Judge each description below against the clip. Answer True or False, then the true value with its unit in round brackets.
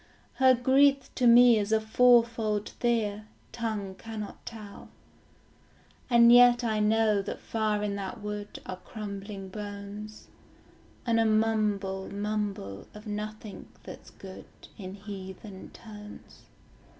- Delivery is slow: True (120 wpm)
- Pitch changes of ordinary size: False (2.1 semitones)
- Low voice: False (210 Hz)